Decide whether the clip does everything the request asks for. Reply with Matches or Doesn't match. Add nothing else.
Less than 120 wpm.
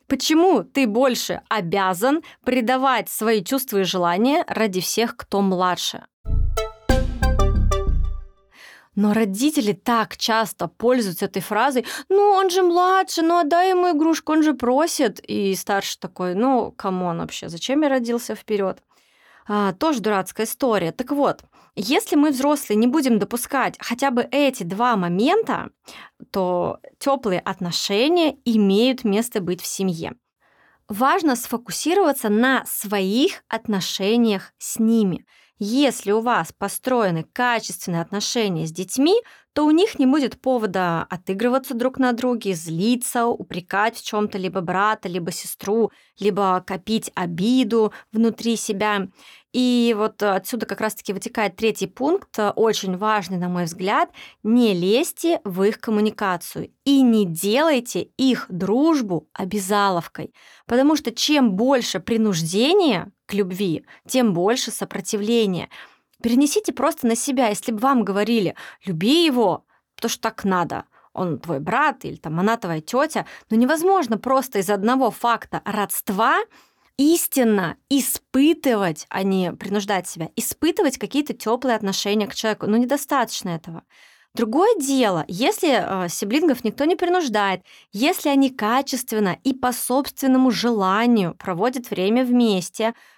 Doesn't match